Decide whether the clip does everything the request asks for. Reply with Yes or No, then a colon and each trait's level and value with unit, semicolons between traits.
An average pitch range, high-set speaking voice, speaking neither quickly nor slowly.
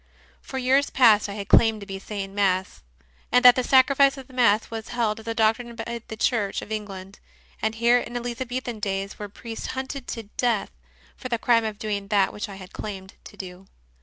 No: average, 3.3 semitones; high, 225 Hz; fast, 210 wpm